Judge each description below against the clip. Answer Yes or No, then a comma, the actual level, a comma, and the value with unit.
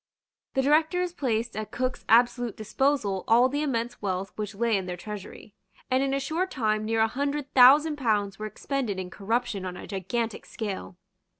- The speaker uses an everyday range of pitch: Yes, average, 4.6 semitones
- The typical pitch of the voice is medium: No, high, 230 Hz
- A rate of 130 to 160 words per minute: No, average, 180 wpm